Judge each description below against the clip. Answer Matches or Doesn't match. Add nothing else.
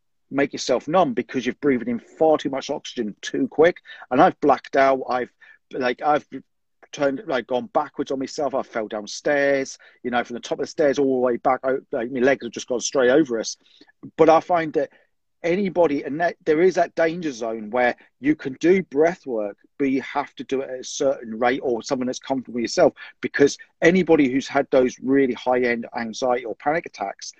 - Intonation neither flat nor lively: Matches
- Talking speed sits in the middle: Doesn't match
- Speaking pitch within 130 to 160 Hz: Matches